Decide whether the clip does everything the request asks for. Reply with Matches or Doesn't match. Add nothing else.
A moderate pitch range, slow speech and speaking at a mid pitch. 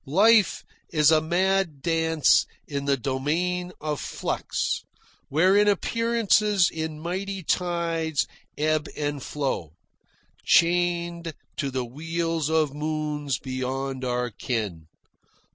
Matches